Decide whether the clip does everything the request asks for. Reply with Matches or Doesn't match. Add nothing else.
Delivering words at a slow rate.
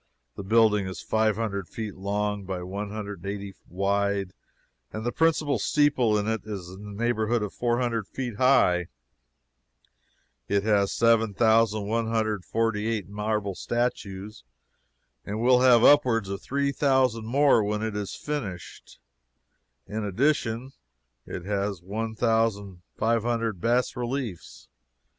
Matches